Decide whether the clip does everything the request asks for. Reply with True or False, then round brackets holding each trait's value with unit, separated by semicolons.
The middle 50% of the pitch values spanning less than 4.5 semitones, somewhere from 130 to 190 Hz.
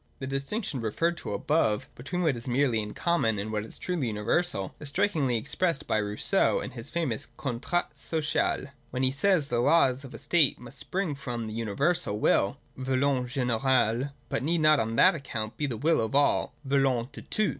False (5.0 semitones; 135 Hz)